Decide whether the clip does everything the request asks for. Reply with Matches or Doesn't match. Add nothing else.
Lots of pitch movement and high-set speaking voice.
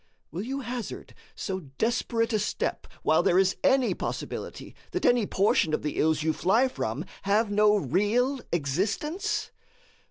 Matches